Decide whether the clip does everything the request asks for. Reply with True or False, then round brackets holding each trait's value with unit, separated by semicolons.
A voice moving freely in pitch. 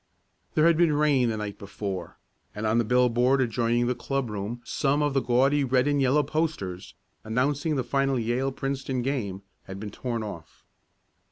False (3.9 semitones)